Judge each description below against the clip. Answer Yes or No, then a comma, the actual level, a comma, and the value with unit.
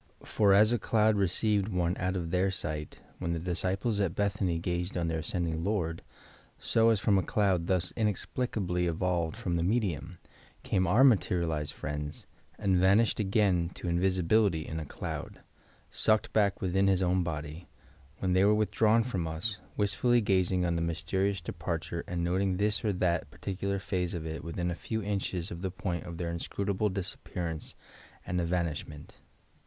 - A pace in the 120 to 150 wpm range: No, average, 170 wpm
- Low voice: Yes, very low, 90 Hz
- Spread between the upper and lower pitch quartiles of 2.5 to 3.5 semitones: Yes, average, 2.9 semitones